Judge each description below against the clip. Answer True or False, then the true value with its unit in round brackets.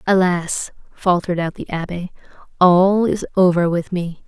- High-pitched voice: False (180 Hz)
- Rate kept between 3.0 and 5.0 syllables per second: True (4.5 syllables/s)